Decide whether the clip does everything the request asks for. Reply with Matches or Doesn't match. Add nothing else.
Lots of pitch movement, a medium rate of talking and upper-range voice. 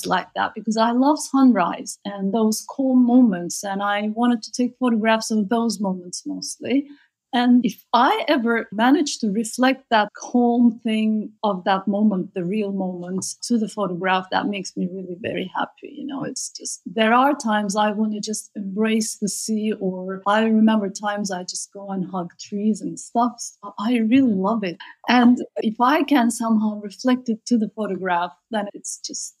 Doesn't match